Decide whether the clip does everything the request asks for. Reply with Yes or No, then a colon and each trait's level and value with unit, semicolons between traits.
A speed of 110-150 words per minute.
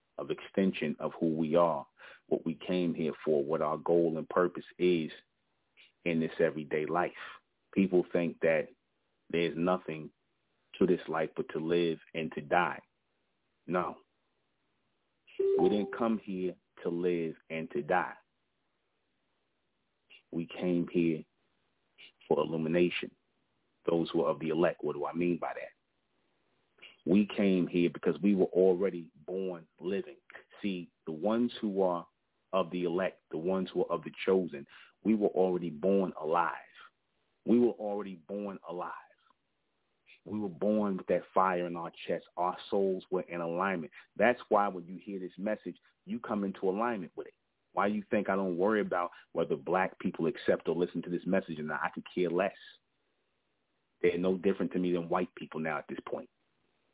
No: average, 165 wpm